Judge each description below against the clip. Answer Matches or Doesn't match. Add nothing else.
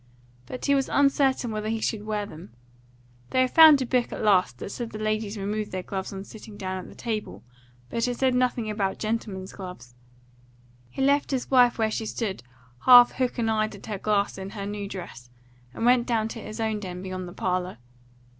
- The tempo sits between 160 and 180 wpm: Doesn't match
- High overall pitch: Matches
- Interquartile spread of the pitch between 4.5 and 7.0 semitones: Doesn't match